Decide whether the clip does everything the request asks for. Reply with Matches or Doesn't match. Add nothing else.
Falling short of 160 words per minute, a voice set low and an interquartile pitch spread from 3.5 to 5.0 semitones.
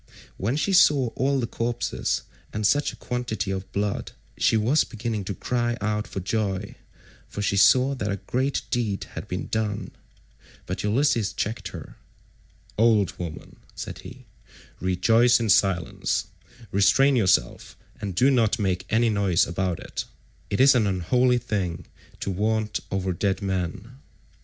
Matches